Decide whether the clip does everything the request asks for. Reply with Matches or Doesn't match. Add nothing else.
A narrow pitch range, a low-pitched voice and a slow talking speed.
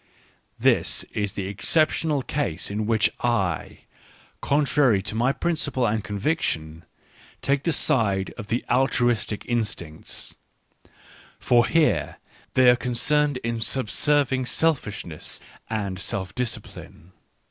Doesn't match